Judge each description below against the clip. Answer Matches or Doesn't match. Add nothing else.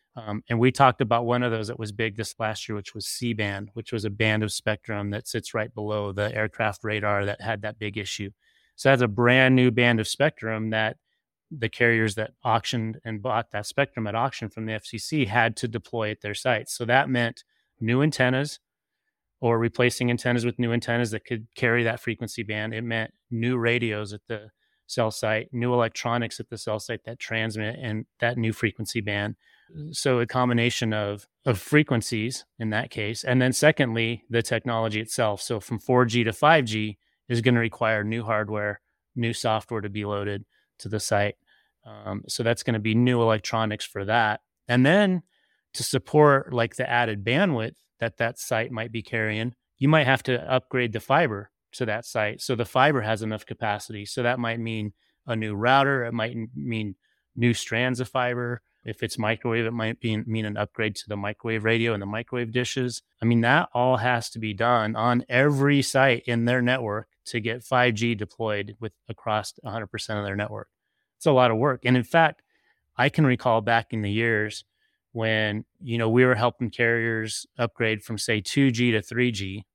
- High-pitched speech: Doesn't match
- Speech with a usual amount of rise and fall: Doesn't match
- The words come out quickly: Doesn't match